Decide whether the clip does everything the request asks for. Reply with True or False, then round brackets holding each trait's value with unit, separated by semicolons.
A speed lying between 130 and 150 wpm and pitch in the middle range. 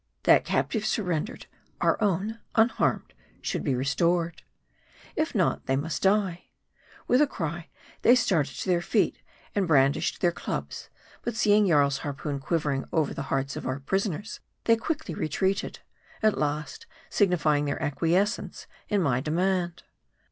True (140 wpm; 170 Hz)